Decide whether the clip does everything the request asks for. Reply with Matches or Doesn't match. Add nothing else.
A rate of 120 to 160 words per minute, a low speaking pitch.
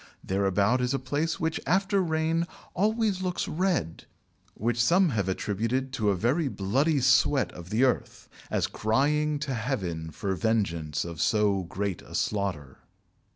Matches